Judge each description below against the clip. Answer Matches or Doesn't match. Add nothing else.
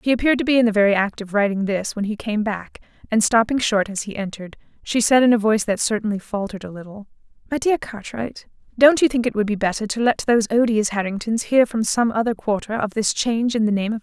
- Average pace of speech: Doesn't match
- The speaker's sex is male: Doesn't match